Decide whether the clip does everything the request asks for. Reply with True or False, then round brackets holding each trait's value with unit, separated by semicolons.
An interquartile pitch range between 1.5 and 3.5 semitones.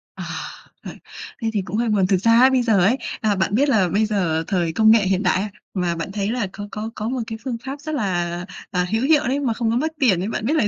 False (4.2 semitones)